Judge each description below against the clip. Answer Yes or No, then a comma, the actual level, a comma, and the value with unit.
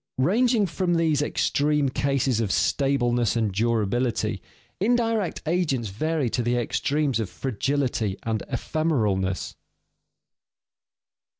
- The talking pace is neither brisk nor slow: No, slow, 100 wpm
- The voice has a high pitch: No, low, 135 Hz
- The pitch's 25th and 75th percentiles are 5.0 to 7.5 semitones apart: Yes, wide, 5.5 semitones